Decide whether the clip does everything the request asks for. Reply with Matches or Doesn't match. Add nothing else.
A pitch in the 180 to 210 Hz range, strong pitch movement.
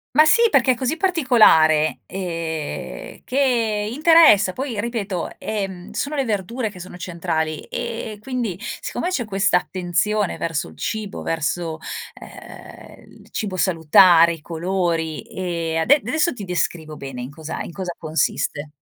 Matches